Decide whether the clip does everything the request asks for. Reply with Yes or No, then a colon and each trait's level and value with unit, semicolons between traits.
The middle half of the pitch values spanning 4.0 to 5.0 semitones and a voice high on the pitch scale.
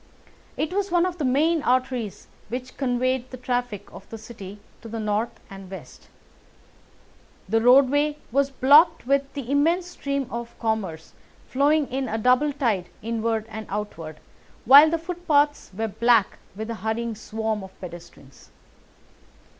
Yes: average, 4.5 semitones; high, 245 Hz